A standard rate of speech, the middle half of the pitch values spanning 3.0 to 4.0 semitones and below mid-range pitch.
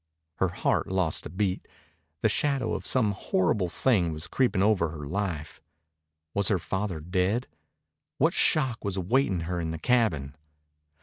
No: average, 150 wpm; average, 4.4 semitones; very low, 95 Hz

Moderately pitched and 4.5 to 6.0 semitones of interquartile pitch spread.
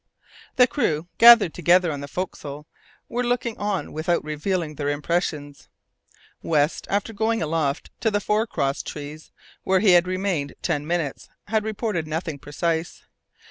Yes: medium, 170 Hz; wide, 5.4 semitones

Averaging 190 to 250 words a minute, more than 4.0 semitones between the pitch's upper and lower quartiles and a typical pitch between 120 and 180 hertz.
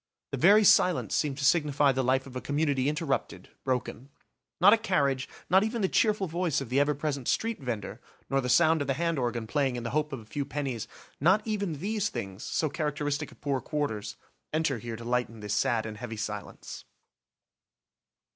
Yes: average, 195 wpm; average, 4.4 semitones; medium, 140 Hz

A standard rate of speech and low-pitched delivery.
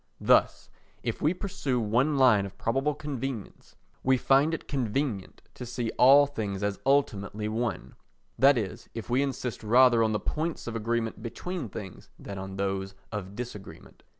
Yes: average, 160 wpm; low, 120 Hz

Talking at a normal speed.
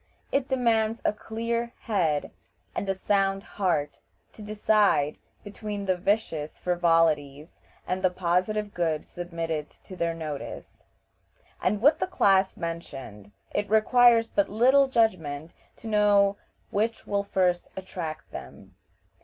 No: slow, 125 wpm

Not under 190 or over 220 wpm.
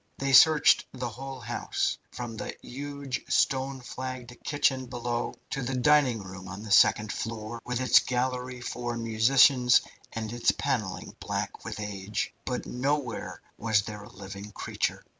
No: average, 150 wpm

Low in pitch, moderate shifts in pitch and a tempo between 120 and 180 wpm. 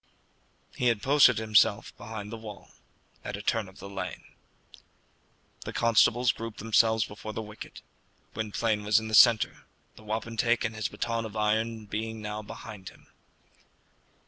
No: low, 110 Hz; narrow, 1.4 semitones; average, 150 wpm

